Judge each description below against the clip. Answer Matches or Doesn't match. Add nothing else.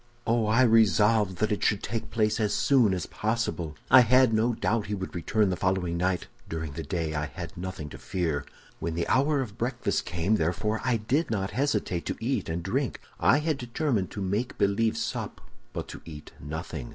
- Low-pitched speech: Matches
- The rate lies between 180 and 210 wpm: Matches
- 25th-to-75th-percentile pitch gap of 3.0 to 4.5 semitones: Doesn't match